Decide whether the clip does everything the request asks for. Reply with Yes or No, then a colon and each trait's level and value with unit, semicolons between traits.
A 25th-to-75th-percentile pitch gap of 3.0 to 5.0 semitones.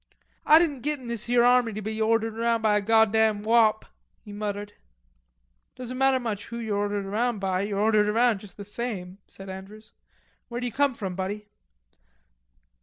No: narrow, 2.6 semitones